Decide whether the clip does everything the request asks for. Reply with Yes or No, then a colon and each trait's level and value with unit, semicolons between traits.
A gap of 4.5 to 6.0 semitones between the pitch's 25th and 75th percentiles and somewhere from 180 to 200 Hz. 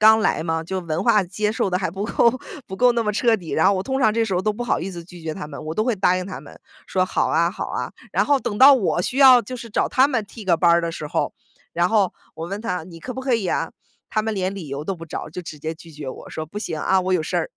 Yes: average, 4.8 semitones; high, 190 Hz